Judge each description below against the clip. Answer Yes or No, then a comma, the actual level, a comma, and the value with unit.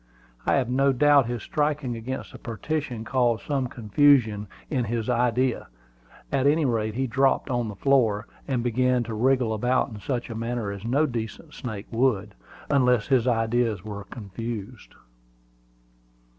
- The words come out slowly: No, average, 155 wpm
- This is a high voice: No, low, 120 Hz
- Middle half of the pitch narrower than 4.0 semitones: Yes, average, 3.0 semitones